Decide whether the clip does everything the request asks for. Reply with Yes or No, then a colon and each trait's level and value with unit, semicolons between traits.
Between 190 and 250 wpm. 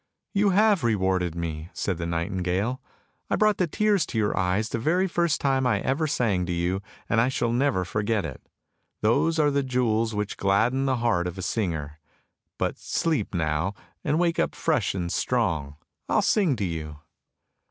Yes: average, 195 wpm